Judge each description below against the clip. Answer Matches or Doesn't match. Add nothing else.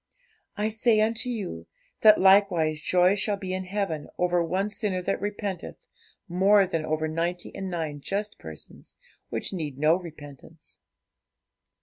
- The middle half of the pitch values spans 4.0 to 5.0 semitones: Matches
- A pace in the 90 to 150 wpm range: Matches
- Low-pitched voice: Doesn't match